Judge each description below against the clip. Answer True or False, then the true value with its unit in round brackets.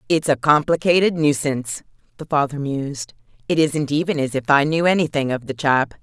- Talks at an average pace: True (180 wpm)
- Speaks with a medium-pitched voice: True (145 Hz)